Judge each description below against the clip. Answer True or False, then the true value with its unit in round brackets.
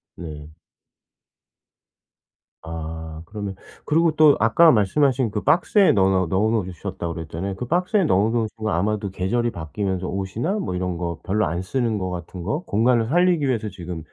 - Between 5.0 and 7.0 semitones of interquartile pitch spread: True (5.4 semitones)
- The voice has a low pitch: True (100 Hz)